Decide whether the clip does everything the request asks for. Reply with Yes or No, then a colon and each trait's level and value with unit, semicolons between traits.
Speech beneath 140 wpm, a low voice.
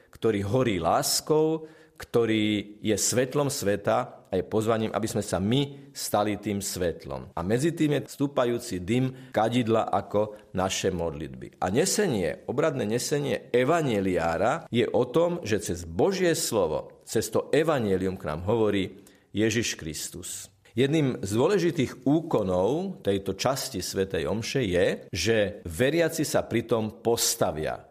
Yes: average, 130 wpm; low, 110 Hz